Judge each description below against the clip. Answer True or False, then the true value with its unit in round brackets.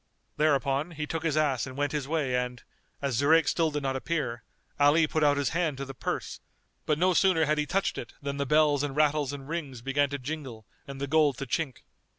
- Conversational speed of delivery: False (225 wpm)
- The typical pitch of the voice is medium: True (145 Hz)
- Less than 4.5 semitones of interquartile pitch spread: True (2.4 semitones)